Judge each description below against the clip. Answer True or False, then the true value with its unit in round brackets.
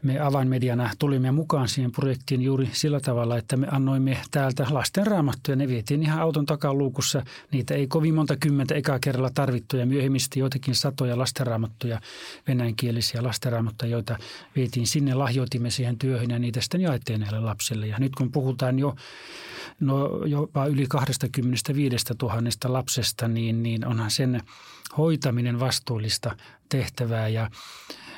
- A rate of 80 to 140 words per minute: True (135 wpm)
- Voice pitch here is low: True (130 Hz)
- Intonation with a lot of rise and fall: False (2.6 semitones)